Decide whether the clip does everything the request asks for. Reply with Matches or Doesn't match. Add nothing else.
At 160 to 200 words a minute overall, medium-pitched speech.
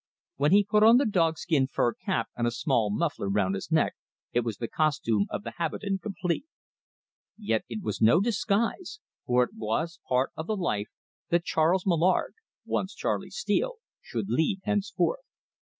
Matches